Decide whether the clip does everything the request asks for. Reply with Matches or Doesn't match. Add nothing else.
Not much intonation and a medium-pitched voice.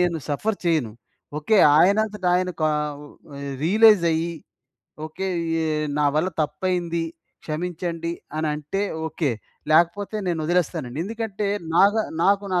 Doesn't match